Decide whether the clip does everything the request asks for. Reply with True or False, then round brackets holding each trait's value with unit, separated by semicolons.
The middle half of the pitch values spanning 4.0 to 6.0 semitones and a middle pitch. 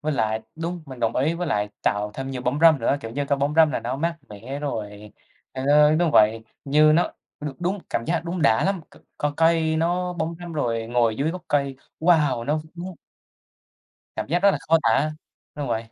True (5.4 semitones; 145 Hz)